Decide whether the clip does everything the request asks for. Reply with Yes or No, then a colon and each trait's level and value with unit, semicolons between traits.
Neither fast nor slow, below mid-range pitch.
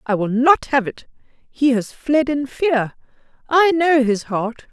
No: average, 180 wpm; very high, 265 Hz